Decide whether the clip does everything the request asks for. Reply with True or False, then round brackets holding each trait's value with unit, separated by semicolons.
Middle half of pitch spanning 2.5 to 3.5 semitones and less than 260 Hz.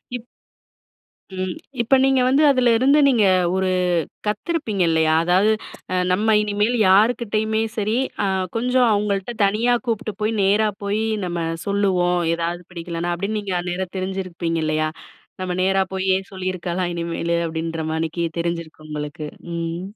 False (4.1 semitones; 190 Hz)